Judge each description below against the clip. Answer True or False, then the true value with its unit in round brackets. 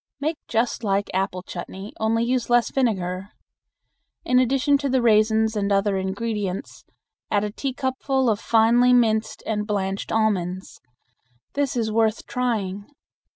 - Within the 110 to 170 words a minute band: True (135 wpm)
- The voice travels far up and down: False (3.7 semitones)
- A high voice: True (220 Hz)